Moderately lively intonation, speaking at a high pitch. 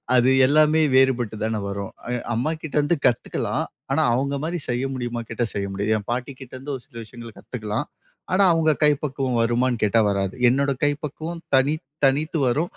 No: average, 3.9 semitones; low, 130 Hz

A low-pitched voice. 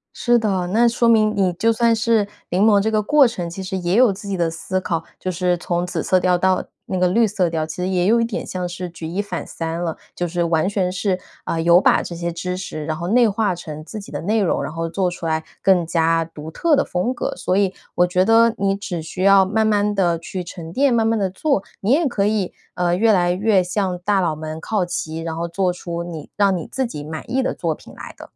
No: medium, 185 Hz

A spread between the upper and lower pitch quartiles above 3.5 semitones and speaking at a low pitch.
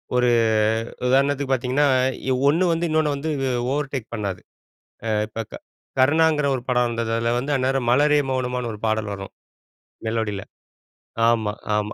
Yes: average, 4.0 semitones; low, 125 Hz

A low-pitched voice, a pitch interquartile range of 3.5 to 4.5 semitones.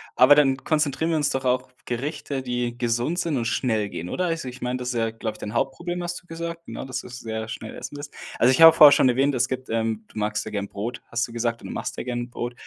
Yes: low, 125 Hz; average, 3.8 semitones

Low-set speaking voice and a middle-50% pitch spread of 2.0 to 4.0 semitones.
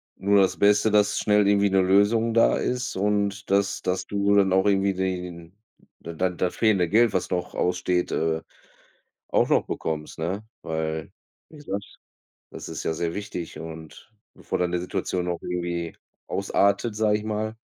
Yes: very low, 95 Hz; average, 2.7 semitones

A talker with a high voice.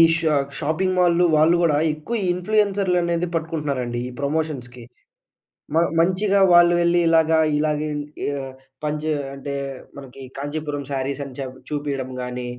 No: medium, 155 Hz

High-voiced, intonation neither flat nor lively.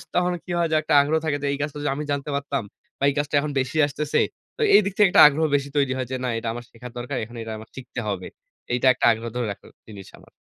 No: medium, 140 Hz; average, 3.8 semitones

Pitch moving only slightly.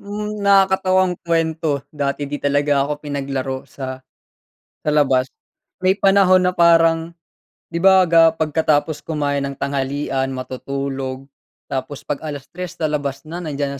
No: average, 3.7 semitones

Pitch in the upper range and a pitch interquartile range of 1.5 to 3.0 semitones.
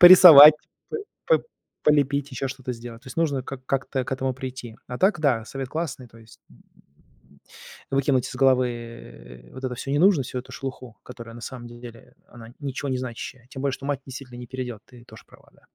No: low, 130 Hz; narrow, 2.4 semitones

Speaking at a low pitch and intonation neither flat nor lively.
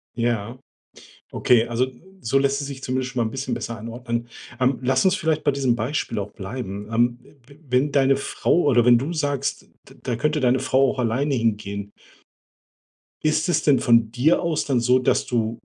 Yes: low, 125 Hz; average, 3.1 semitones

